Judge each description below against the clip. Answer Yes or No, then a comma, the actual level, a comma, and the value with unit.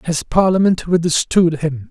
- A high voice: No, medium, 165 Hz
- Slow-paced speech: Yes, slow, 125 wpm